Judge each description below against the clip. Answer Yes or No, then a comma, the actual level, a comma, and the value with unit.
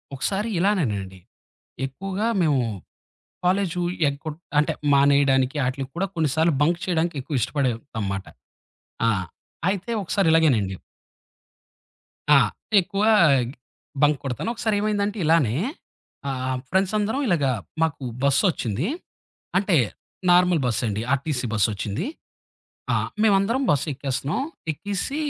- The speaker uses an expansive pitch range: Yes, wide, 6.7 semitones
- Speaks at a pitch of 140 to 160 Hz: Yes, medium, 155 Hz